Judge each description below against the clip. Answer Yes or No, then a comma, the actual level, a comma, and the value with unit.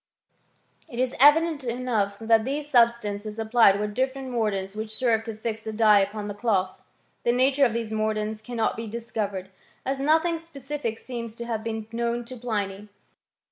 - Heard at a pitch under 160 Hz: No, high, 230 Hz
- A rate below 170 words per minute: No, average, 175 wpm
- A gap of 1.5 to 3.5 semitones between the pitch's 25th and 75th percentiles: Yes, average, 2.9 semitones